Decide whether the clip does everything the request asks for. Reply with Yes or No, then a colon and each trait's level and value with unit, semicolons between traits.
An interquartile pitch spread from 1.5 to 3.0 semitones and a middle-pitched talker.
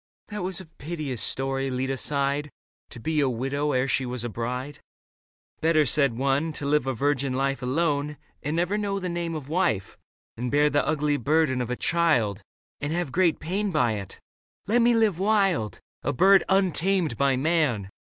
No: average, 4.7 semitones; medium, 145 Hz